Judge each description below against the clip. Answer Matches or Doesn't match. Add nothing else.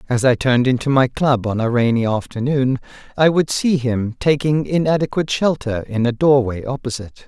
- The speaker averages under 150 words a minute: Doesn't match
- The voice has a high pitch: Doesn't match